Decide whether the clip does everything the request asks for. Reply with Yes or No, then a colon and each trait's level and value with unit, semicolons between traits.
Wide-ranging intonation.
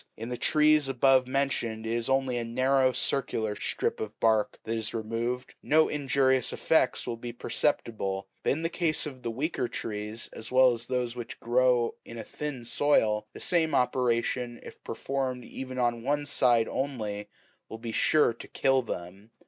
No: average, 2.9 semitones